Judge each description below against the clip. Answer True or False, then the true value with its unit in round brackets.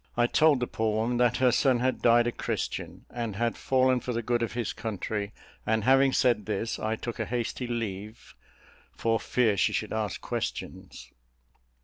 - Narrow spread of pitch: True (2.0 semitones)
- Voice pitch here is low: True (120 Hz)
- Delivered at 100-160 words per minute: False (180 wpm)